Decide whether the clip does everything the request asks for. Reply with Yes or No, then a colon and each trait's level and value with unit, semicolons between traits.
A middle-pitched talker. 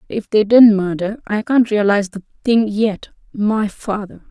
No: high, 210 Hz